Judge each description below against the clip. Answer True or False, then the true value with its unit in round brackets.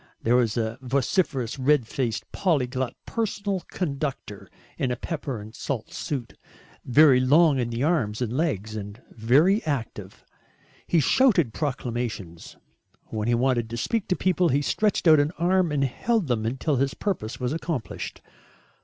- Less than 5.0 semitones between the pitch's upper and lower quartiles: False (5.6 semitones)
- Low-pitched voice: True (130 Hz)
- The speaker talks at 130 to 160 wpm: True (155 wpm)